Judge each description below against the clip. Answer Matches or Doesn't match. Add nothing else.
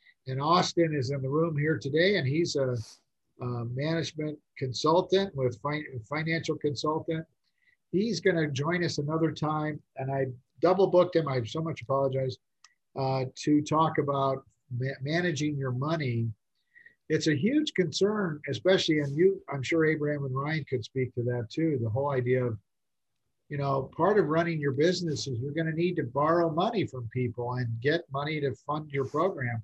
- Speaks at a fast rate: Doesn't match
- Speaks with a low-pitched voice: Doesn't match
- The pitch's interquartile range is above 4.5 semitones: Doesn't match